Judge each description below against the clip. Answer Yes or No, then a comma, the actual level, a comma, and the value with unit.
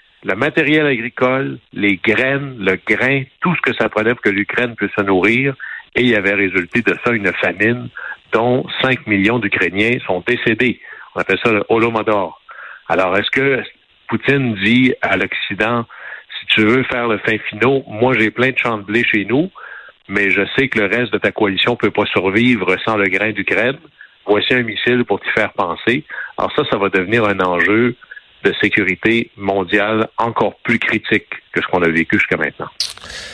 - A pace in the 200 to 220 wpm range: No, average, 185 wpm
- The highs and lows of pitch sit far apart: No, average, 3.5 semitones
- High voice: No, low, 115 Hz